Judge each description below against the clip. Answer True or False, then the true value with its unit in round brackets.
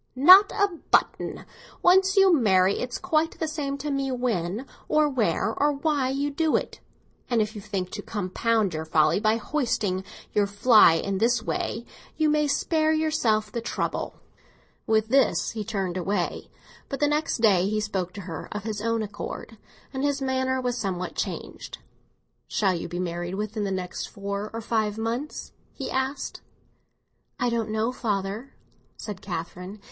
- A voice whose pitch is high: True (225 Hz)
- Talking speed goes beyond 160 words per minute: True (170 wpm)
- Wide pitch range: True (5.7 semitones)